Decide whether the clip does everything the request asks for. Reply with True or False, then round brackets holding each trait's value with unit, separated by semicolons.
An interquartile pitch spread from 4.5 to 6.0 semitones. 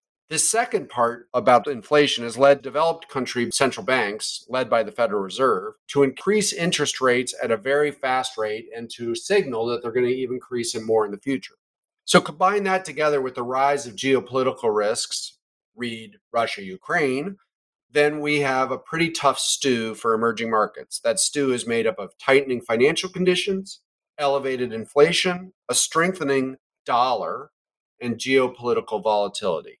True (5.3 semitones)